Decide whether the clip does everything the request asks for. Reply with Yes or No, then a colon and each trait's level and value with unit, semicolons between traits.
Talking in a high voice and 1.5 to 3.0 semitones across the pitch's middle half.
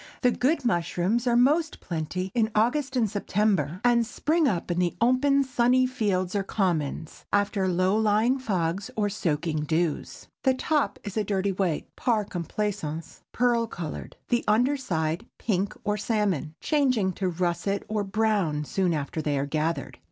No: high, 205 Hz; wide, 5.5 semitones